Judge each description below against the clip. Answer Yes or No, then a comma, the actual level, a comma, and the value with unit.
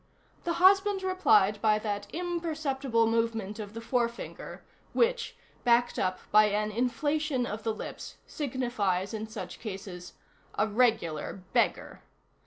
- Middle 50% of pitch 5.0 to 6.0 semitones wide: Yes, average, 5.3 semitones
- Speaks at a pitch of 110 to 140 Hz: No, high, 230 Hz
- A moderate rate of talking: No, slow, 125 wpm